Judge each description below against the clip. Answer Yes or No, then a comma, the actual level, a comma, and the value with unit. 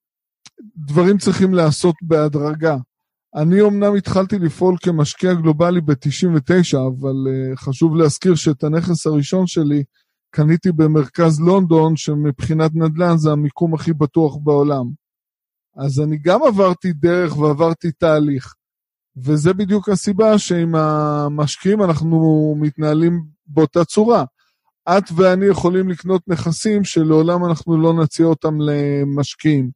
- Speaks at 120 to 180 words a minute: No, average, 110 wpm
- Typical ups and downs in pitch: Yes, average, 3.0 semitones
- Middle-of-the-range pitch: Yes, medium, 160 Hz